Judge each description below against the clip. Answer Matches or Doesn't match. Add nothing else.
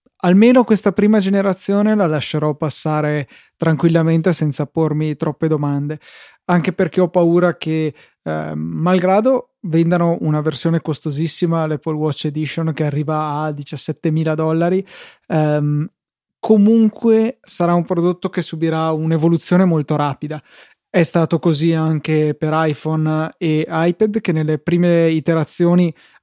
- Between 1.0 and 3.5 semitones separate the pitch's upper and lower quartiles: Matches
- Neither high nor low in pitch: Matches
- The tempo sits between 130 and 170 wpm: Doesn't match